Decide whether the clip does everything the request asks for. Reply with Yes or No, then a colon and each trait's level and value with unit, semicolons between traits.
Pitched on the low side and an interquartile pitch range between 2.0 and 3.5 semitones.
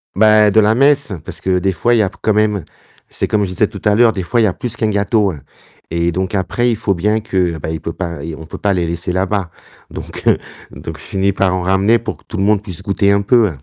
Yes: low, 100 Hz; average, 2.8 semitones